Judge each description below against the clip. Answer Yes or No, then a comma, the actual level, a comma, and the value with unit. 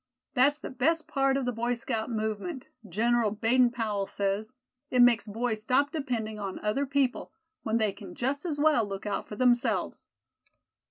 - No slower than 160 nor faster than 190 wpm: Yes, average, 170 wpm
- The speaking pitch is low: No, high, 240 Hz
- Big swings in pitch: No, average, 3.8 semitones